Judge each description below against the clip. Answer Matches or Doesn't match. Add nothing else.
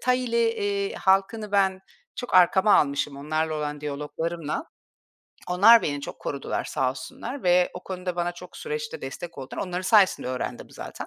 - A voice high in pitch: Doesn't match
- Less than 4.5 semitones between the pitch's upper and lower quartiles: Doesn't match